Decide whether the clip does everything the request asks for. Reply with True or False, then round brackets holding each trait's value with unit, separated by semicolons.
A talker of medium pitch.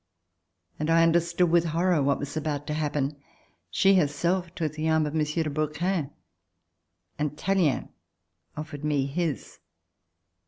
True (155 Hz)